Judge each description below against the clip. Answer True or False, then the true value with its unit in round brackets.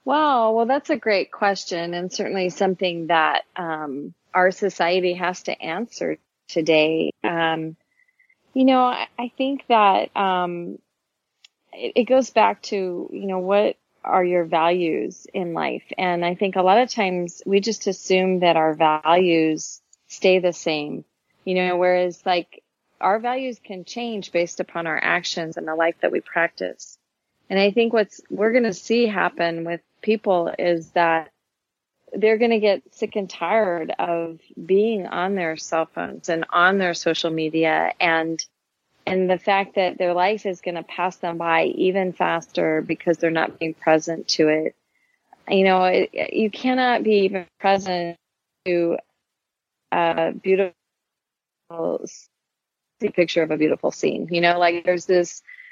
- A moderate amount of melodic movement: True (3.3 semitones)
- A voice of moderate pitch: True (180 Hz)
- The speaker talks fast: False (155 wpm)